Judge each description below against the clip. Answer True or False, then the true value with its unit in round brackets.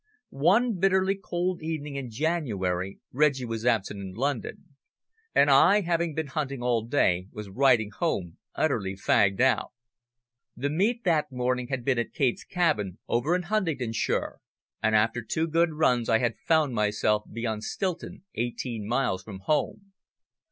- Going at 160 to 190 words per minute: False (150 wpm)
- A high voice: False (130 Hz)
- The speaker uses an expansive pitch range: True (6.6 semitones)